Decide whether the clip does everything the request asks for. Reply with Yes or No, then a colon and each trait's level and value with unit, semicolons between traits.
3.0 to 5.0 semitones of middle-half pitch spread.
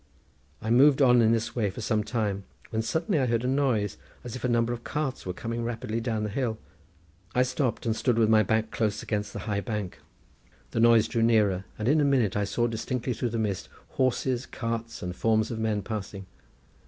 No: narrow, 2.4 semitones